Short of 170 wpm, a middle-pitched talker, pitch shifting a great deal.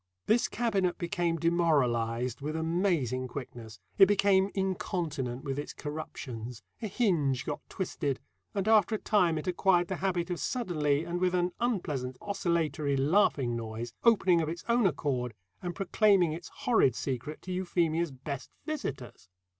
Yes: average, 145 wpm; medium, 165 Hz; wide, 5.9 semitones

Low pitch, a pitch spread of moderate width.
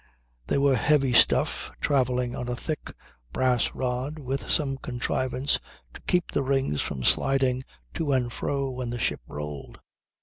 No: low, 130 Hz; narrow, 1.9 semitones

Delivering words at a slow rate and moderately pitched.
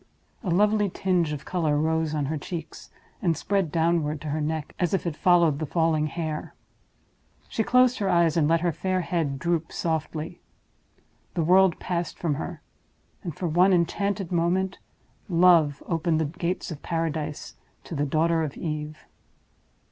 No: average, 165 wpm; medium, 165 Hz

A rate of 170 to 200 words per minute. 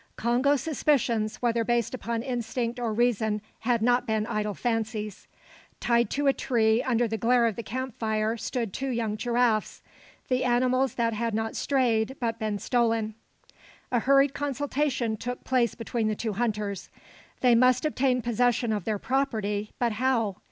No: average, 160 wpm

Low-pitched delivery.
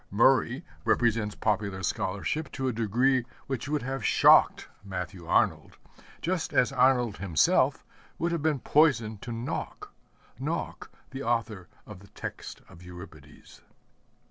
Yes: low, 115 Hz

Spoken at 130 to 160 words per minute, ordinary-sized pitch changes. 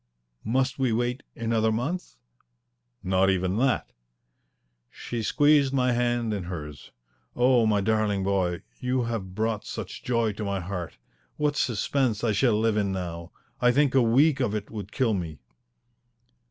Yes: average, 155 wpm; average, 4.2 semitones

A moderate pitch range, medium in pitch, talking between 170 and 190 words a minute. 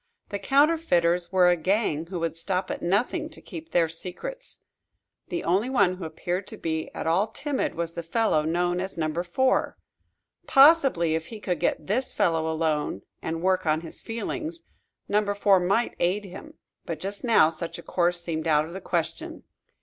Yes: average, 4.3 semitones; medium, 180 Hz; average, 180 wpm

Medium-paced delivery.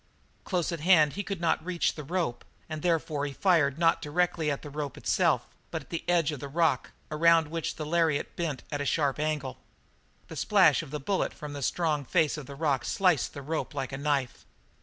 No: fast, 215 wpm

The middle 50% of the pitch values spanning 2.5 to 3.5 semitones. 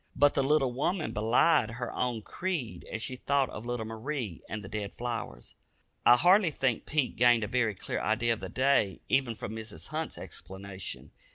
No: average, 4.0 semitones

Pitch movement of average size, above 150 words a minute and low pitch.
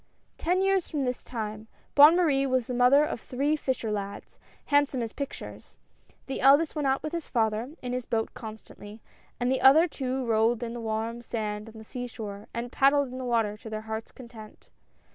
No: average, 3.8 semitones; average, 200 wpm; high, 245 Hz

